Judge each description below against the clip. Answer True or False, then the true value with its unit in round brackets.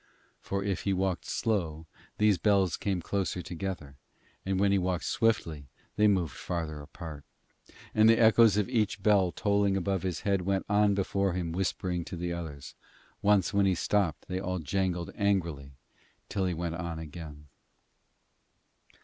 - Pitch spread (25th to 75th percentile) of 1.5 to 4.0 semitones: True (3.0 semitones)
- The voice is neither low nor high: False (95 Hz)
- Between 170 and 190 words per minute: False (160 wpm)